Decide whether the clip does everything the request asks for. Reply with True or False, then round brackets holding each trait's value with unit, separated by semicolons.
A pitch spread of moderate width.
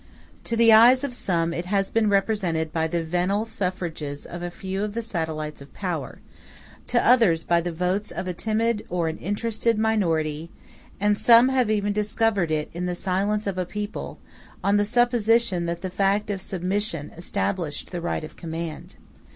True (4.2 semitones)